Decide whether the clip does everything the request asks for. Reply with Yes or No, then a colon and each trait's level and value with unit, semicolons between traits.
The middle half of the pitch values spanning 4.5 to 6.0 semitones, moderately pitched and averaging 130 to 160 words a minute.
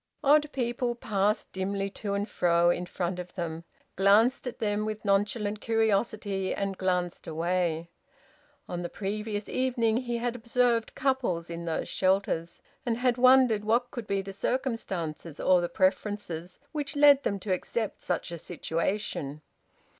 No: average, 4.8 semitones; high, 205 Hz; average, 150 wpm